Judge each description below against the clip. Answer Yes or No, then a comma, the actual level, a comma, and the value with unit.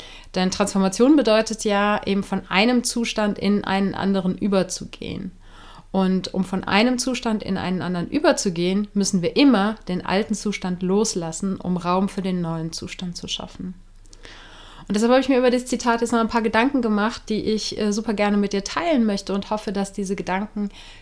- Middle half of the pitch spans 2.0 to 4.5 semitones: Yes, average, 2.8 semitones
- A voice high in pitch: Yes, high, 200 Hz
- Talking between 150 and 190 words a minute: Yes, average, 180 wpm